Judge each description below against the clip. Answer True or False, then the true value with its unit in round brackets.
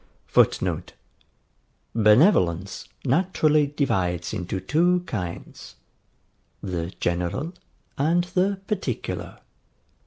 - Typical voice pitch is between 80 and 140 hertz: True (135 Hz)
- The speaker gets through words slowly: True (70 wpm)